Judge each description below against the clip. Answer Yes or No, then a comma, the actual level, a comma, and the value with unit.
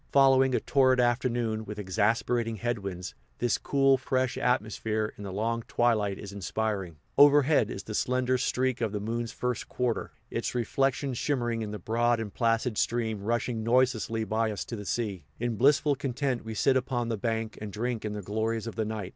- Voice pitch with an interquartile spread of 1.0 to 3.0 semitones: Yes, narrow, 2.6 semitones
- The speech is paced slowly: No, average, 185 wpm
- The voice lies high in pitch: No, low, 115 Hz